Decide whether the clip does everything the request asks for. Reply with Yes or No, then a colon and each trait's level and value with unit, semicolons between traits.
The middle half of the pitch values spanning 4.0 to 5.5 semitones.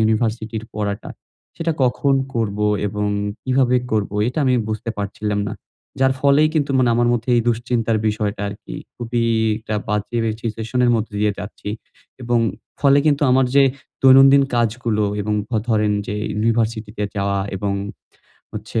No: average, 3.1 semitones